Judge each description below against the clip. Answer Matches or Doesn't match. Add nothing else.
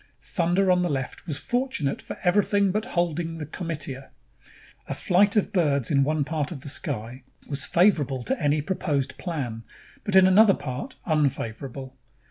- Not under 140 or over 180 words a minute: Matches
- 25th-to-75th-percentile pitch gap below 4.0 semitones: Doesn't match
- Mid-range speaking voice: Matches